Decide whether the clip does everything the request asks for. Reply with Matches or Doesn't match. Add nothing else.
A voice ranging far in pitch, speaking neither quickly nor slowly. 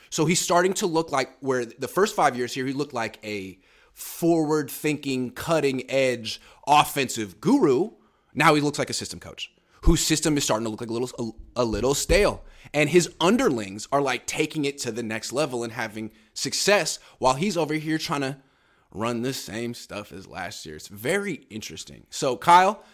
Matches